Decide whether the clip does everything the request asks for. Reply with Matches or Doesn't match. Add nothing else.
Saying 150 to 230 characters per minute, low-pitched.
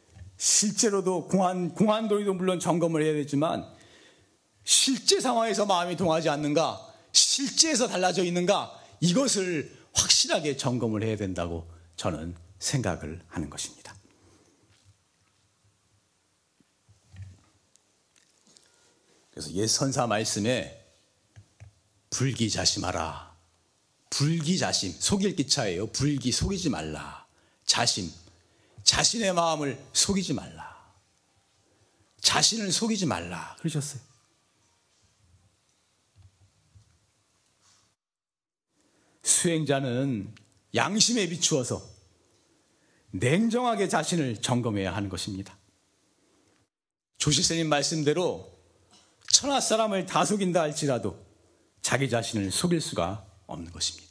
Matches